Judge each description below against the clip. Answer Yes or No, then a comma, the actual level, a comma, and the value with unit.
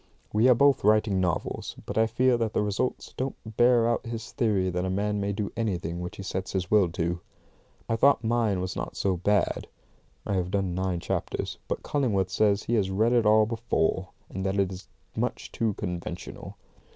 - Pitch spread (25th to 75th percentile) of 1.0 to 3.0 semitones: No, average, 3.5 semitones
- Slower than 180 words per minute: No, average, 200 wpm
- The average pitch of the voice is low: Yes, low, 105 Hz